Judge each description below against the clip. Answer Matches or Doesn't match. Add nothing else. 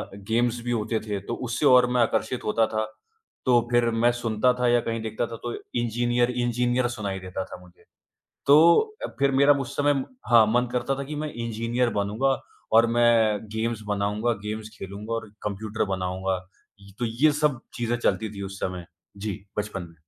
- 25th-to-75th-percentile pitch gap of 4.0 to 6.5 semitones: Doesn't match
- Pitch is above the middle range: Doesn't match